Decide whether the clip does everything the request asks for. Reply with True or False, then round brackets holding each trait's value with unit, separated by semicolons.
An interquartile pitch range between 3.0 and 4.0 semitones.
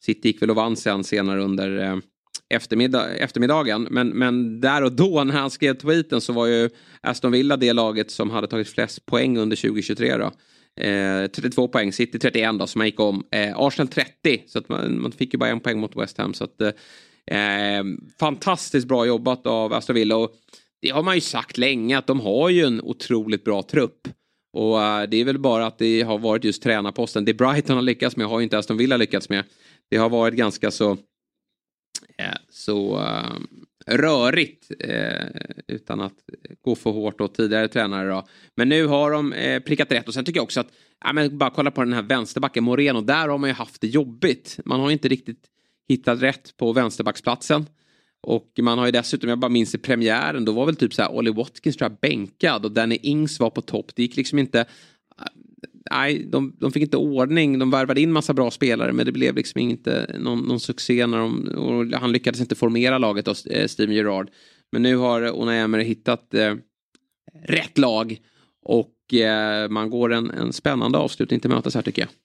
True (3.5 semitones)